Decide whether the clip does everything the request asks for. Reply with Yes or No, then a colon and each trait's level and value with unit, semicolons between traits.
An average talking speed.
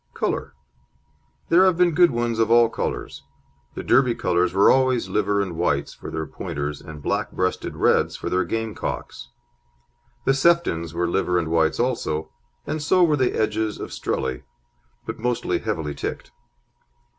Yes: average, 160 wpm